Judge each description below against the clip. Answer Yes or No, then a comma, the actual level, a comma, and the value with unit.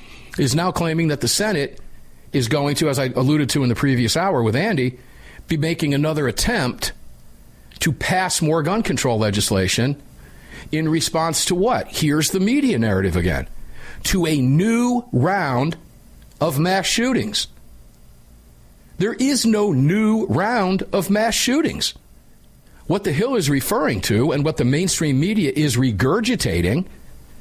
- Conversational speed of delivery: Yes, average, 145 wpm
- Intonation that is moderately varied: No, wide, 7.4 semitones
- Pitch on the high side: No, medium, 150 Hz